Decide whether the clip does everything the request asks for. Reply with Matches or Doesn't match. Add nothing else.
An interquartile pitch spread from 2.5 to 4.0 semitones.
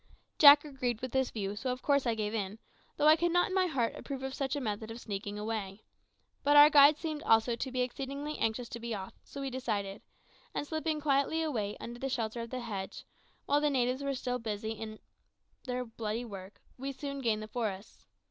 Doesn't match